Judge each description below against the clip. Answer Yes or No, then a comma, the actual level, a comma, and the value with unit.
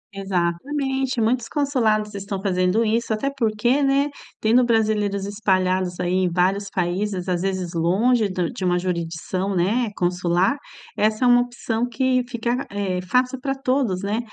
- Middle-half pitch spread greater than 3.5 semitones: Yes, average, 4.9 semitones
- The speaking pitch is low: No, high, 210 Hz